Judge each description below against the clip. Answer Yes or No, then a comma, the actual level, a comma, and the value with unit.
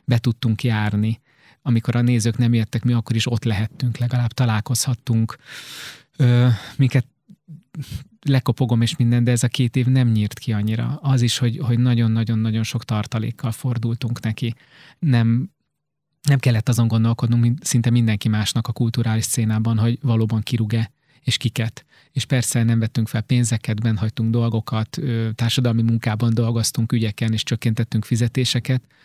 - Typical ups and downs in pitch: No, narrow, 1.8 semitones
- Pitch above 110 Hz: Yes, low, 120 Hz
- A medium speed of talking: Yes, average, 145 wpm